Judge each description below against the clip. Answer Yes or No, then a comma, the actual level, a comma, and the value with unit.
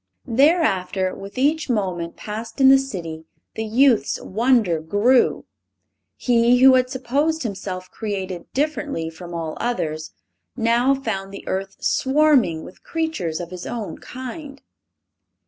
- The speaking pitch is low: No, high, 225 Hz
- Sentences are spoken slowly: Yes, slow, 130 wpm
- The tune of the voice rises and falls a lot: Yes, wide, 6.3 semitones